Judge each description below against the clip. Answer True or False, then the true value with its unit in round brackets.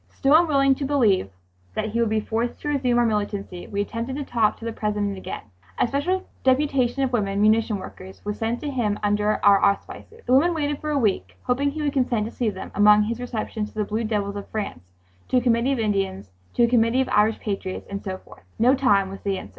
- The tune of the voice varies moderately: True (4.2 semitones)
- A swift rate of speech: True (230 wpm)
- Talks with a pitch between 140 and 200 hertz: False (225 Hz)